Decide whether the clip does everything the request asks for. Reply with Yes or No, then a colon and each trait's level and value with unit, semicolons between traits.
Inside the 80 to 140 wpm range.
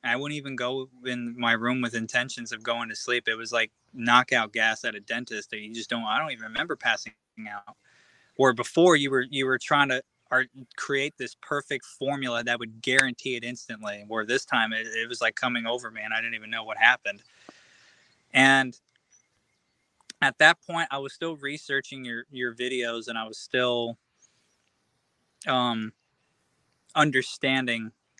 No: average, 175 wpm